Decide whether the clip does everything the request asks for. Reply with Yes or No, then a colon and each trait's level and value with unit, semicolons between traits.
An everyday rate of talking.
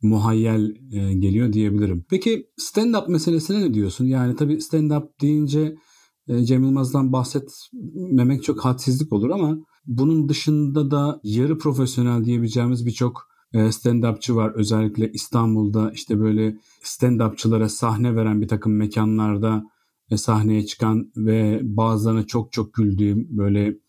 Yes: average, 115 wpm